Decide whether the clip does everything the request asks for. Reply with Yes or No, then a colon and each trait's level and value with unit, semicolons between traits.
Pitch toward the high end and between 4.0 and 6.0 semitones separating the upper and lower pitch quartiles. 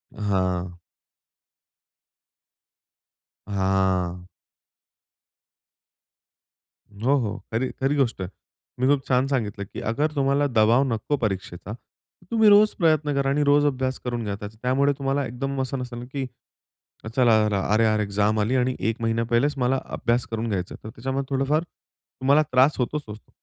No: low, 125 Hz; average, 4.4 semitones